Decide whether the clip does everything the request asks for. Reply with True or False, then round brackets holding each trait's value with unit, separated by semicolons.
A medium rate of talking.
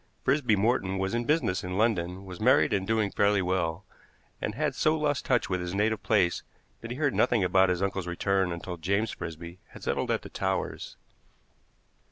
True (190 wpm)